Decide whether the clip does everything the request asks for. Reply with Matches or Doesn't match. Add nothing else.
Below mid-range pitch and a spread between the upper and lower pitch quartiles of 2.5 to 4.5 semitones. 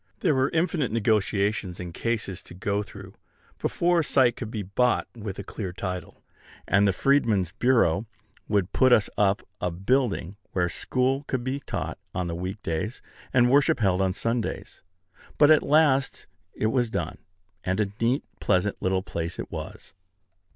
Doesn't match